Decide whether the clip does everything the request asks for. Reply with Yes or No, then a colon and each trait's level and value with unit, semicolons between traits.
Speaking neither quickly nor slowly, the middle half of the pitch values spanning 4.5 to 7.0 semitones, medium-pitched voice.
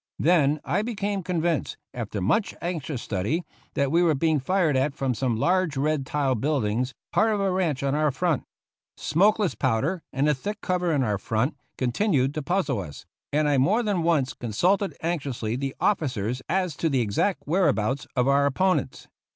Yes: average, 180 wpm; wide, 5.5 semitones; medium, 150 Hz